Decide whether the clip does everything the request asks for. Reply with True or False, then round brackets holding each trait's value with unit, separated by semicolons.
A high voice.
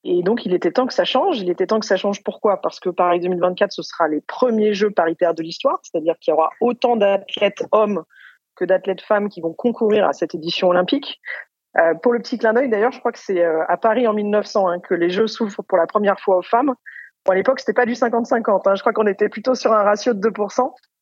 True (205 Hz)